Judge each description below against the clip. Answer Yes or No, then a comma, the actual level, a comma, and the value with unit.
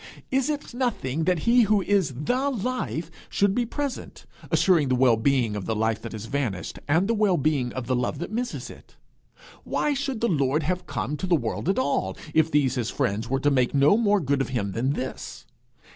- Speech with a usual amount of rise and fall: No, wide, 8.5 semitones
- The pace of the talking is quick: Yes, fast, 215 wpm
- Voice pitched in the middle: Yes, medium, 150 Hz